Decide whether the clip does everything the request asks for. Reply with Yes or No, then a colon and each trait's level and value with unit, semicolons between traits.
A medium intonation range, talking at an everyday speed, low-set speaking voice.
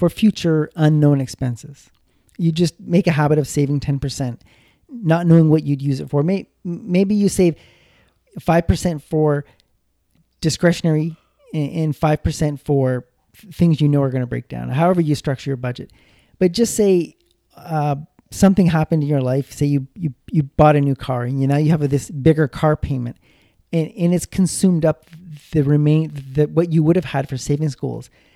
No: average, 3.2 semitones; average, 175 wpm; medium, 150 Hz